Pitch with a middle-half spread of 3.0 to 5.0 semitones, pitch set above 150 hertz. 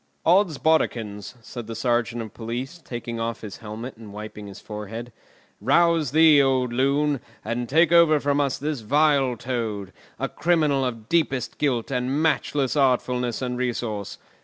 No: average, 4.1 semitones; low, 125 Hz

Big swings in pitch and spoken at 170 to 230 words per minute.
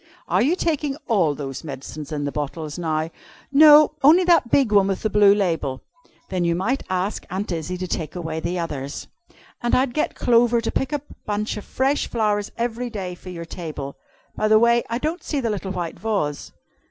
Yes: wide, 6.5 semitones; average, 200 wpm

